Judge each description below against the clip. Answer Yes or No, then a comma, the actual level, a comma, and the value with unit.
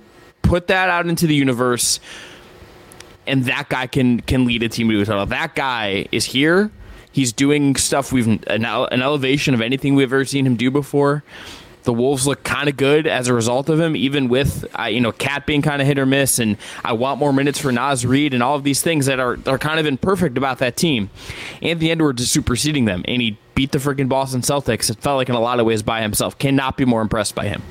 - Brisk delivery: Yes, fast, 235 wpm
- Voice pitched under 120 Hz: No, low, 135 Hz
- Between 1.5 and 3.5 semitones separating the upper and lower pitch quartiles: Yes, average, 3.1 semitones